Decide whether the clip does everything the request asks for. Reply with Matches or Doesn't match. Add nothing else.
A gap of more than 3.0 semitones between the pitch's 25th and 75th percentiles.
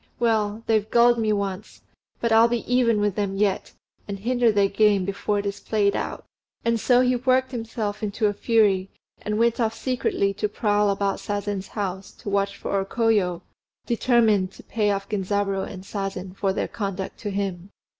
Doesn't match